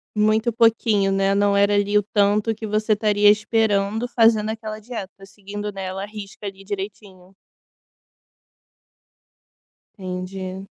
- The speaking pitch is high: Yes, high, 205 Hz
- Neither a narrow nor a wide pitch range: No, narrow, 1.7 semitones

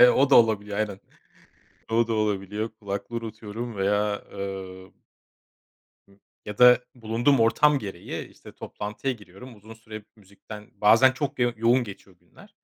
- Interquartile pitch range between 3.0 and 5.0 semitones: No, narrow, 2.6 semitones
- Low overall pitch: Yes, low, 110 Hz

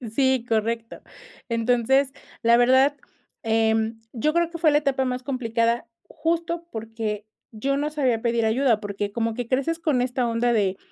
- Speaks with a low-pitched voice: No, high, 240 Hz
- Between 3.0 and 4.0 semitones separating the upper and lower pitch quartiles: Yes, average, 3.5 semitones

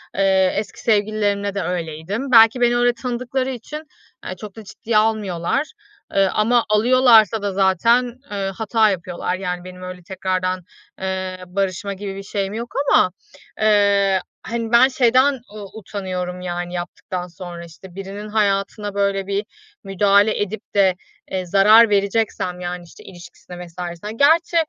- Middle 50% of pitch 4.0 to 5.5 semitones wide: No, average, 3.2 semitones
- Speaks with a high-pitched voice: Yes, high, 200 Hz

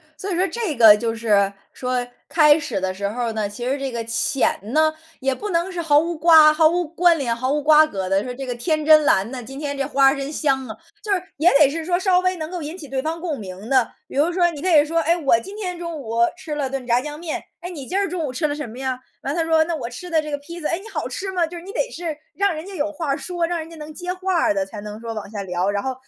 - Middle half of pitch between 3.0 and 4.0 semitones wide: No, average, 5.1 semitones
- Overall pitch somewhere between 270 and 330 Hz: Yes, very high, 300 Hz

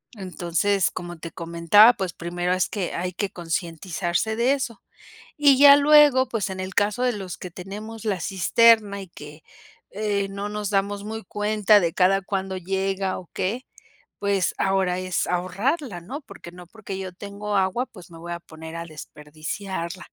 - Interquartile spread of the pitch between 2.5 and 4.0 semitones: Yes, average, 3.2 semitones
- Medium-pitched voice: No, high, 195 Hz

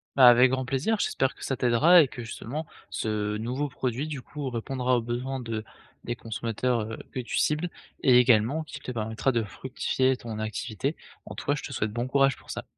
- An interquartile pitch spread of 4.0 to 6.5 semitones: No, average, 2.9 semitones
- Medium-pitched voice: No, low, 125 Hz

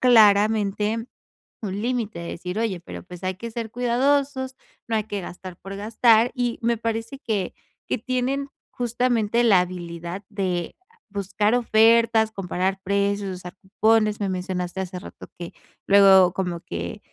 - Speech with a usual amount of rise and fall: Yes, average, 3.7 semitones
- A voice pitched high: Yes, high, 210 Hz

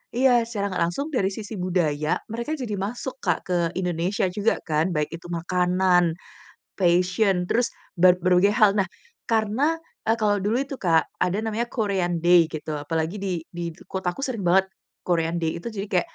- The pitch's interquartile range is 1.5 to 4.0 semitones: Yes, average, 3.7 semitones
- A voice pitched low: No, medium, 185 Hz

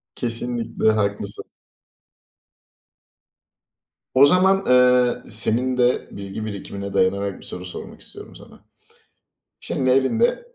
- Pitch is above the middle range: No, low, 120 Hz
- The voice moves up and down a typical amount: Yes, average, 4.2 semitones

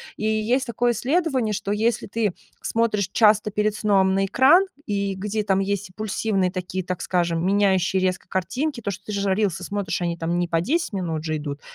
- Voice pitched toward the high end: Yes, high, 200 Hz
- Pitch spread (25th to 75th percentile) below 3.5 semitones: Yes, average, 2.9 semitones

